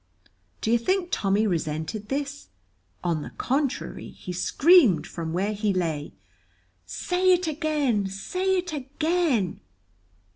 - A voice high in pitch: Yes, high, 235 Hz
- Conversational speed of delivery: No, slow, 120 wpm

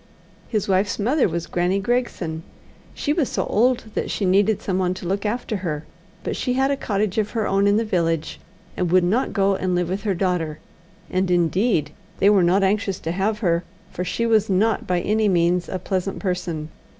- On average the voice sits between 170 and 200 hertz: Yes, high, 190 Hz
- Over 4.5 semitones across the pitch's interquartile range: No, average, 3.1 semitones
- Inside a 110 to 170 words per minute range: No, average, 200 wpm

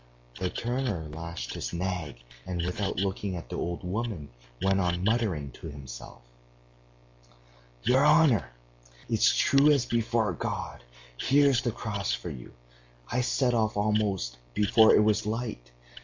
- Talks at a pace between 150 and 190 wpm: No, average, 140 wpm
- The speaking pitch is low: Yes, low, 100 Hz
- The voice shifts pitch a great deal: Yes, wide, 5.7 semitones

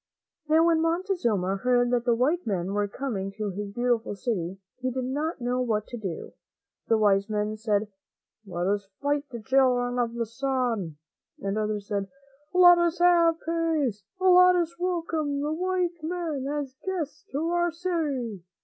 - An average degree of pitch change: No, wide, 7.6 semitones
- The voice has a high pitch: Yes, very high, 255 Hz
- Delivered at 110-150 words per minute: No, average, 175 wpm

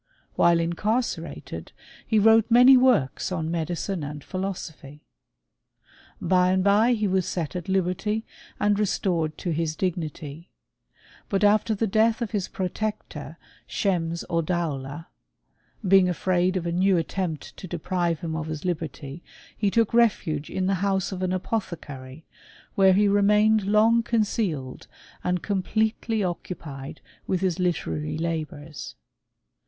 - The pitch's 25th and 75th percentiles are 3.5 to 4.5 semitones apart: Yes, average, 4.0 semitones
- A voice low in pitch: No, medium, 185 Hz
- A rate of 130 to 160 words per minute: Yes, average, 140 wpm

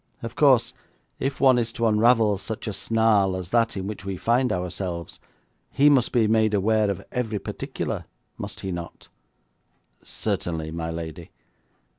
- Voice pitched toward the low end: Yes, low, 105 Hz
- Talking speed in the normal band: Yes, average, 155 wpm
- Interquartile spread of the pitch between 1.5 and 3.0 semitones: No, average, 3.9 semitones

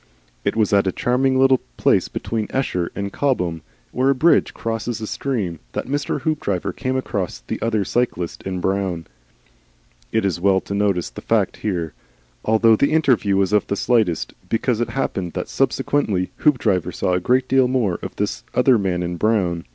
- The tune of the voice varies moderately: No, wide, 5.7 semitones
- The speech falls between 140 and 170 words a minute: No, average, 180 wpm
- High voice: No, low, 105 Hz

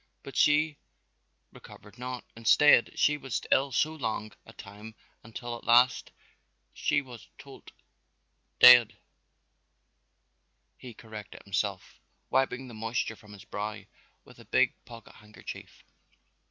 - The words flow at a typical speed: No, slow, 120 wpm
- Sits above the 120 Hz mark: No, low, 115 Hz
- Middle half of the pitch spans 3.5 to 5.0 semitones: No, average, 3.0 semitones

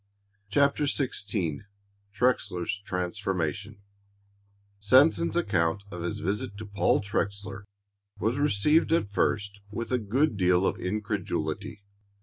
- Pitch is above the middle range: No, low, 100 Hz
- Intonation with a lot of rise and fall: No, average, 3.5 semitones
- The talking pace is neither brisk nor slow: No, slow, 110 wpm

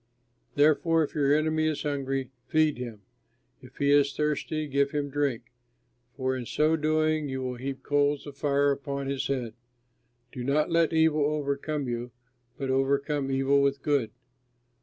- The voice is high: No, medium, 140 Hz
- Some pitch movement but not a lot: No, narrow, 2.0 semitones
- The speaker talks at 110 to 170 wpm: Yes, average, 160 wpm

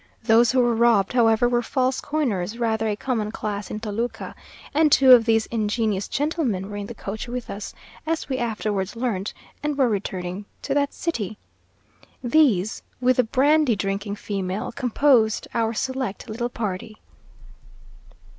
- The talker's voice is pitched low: No, high, 225 Hz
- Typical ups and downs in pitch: Yes, average, 3.6 semitones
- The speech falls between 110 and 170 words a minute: Yes, average, 155 wpm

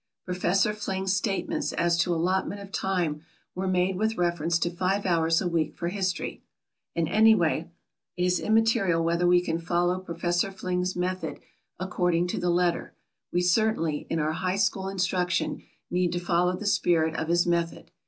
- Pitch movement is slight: Yes, narrow, 1.8 semitones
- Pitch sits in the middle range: Yes, medium, 180 Hz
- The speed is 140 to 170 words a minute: Yes, average, 165 wpm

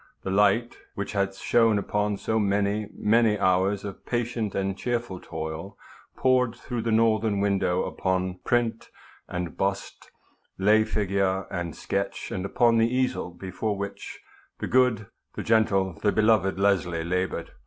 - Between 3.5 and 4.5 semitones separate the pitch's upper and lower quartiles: No, average, 2.8 semitones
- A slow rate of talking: No, average, 145 wpm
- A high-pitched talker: No, low, 100 Hz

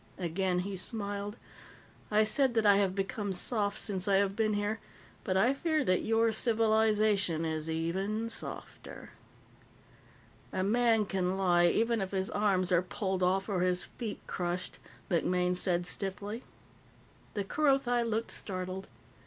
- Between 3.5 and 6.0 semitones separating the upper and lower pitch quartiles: No, average, 3.1 semitones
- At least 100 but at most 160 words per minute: Yes, average, 145 wpm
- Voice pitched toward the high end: Yes, high, 200 Hz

